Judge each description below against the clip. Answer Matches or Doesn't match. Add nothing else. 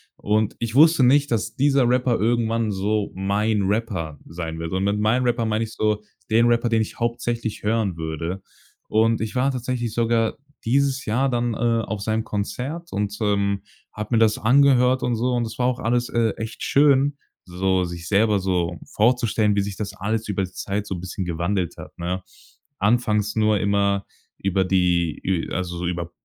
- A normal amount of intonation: Matches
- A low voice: Matches